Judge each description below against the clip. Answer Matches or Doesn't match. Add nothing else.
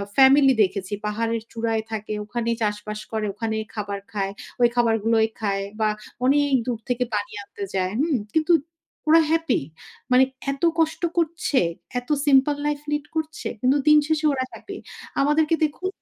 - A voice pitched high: Matches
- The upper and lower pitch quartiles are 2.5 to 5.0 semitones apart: Doesn't match